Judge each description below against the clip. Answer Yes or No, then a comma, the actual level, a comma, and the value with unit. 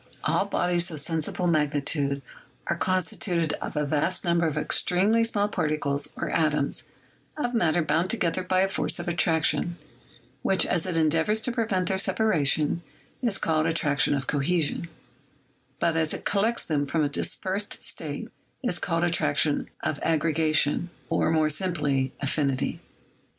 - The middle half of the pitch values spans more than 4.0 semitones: No, average, 3.5 semitones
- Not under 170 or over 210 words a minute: No, average, 150 wpm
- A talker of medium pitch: Yes, medium, 165 Hz